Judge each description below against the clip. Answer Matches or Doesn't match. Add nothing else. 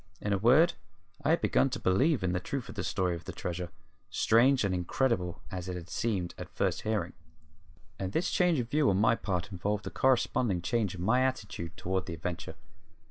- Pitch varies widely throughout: Matches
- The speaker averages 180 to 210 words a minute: Matches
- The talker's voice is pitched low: Matches